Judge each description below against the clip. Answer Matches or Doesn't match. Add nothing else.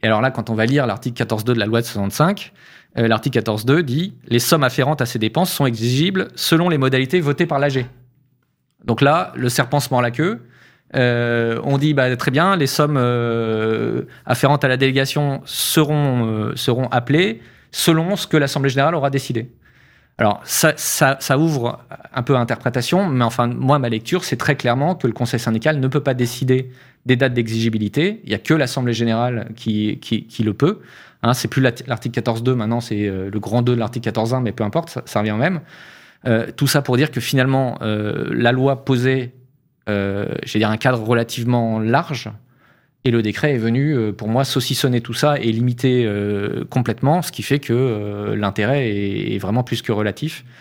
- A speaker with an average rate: Matches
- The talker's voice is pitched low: Matches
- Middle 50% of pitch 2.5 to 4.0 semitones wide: Matches